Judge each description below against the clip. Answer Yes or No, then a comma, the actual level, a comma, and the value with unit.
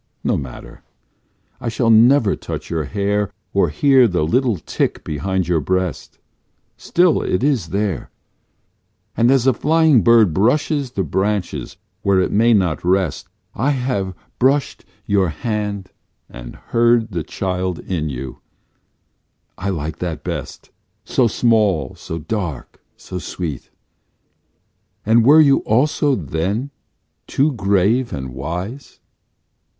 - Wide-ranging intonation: Yes, wide, 5.7 semitones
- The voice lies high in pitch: No, low, 100 Hz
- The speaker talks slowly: Yes, slow, 125 wpm